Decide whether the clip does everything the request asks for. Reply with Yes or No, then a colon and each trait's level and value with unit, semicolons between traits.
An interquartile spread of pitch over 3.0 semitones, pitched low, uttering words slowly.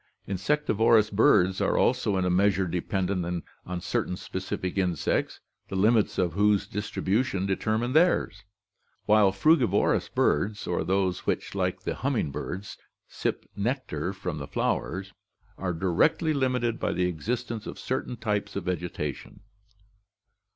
Yes: average, 3.6 semitones; low, 100 Hz; slow, 130 wpm